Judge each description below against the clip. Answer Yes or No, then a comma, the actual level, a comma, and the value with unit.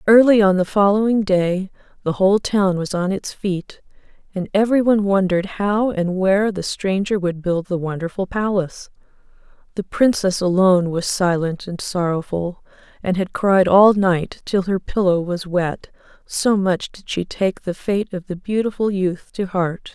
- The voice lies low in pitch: No, high, 190 Hz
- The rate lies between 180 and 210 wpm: No, average, 165 wpm